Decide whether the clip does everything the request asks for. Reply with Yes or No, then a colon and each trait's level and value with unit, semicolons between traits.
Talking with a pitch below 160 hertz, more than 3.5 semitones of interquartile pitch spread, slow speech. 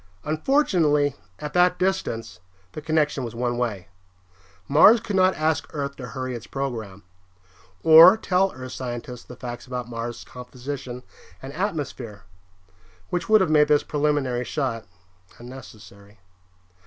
Yes: low, 135 Hz; average, 4.6 semitones; slow, 130 wpm